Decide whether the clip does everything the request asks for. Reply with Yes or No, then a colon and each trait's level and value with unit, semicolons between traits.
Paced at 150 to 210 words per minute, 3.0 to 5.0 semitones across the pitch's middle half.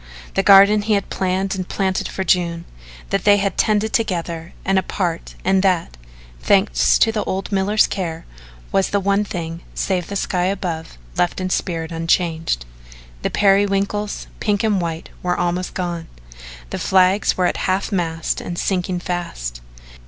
No: average, 160 wpm; narrow, 2.5 semitones